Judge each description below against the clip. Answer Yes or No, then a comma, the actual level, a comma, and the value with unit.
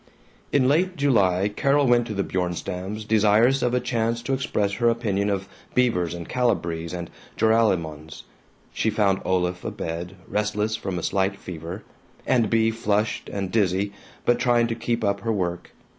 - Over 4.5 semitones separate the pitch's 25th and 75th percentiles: No, average, 4.1 semitones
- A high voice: No, low, 105 Hz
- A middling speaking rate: Yes, average, 160 wpm